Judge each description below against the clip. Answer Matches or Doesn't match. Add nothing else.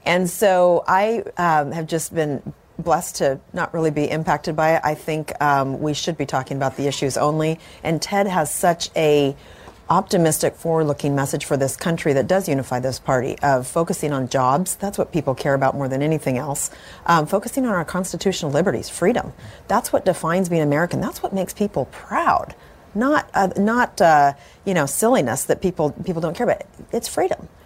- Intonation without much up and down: Doesn't match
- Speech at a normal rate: Matches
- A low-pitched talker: Doesn't match